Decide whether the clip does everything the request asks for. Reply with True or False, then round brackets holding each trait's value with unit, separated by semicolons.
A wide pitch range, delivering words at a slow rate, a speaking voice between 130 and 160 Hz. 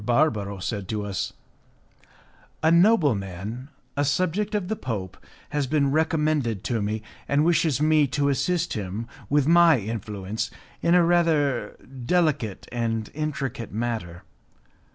True (6.4 semitones; 130 wpm; 135 Hz)